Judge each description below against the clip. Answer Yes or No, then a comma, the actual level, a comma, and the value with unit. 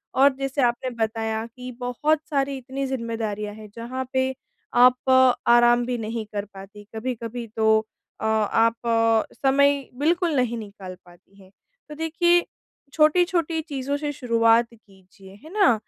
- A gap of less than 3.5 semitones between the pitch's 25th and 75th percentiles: No, average, 4.0 semitones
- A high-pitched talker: Yes, high, 245 Hz